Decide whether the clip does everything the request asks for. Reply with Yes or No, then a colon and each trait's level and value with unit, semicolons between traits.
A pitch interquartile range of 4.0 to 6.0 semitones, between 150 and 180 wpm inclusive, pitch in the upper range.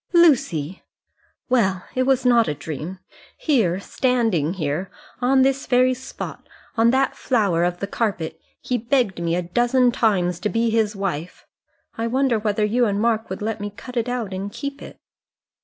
Yes: average, 4.9 semitones; average, 175 wpm; high, 220 Hz